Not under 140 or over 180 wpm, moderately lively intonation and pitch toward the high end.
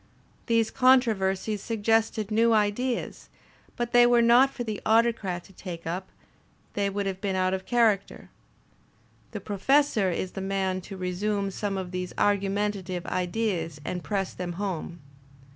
Yes: average, 145 wpm; average, 3.3 semitones; high, 200 Hz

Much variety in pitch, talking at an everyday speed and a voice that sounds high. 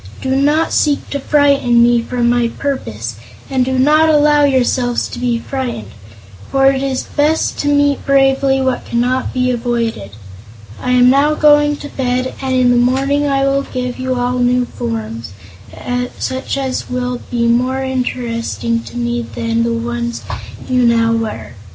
No: narrow, 2.5 semitones; average, 165 wpm; very high, 255 Hz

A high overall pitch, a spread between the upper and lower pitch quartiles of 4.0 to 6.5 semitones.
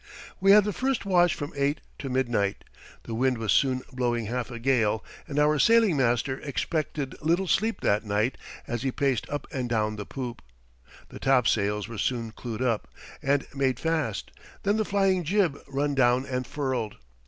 No: low, 130 Hz; average, 4.3 semitones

